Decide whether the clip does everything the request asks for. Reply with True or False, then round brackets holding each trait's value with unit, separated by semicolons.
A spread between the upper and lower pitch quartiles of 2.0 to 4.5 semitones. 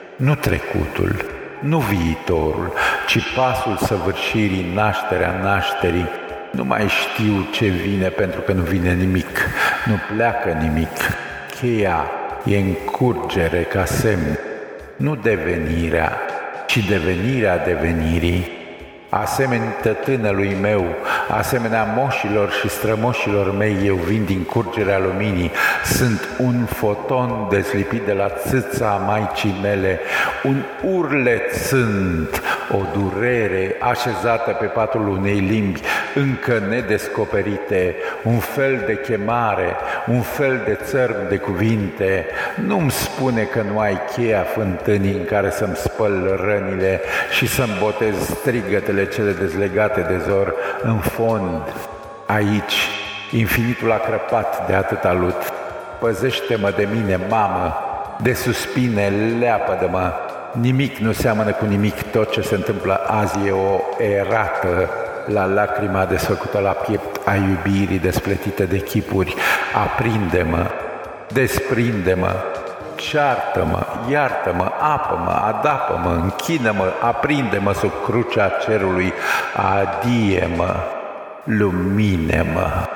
True (2.9 semitones)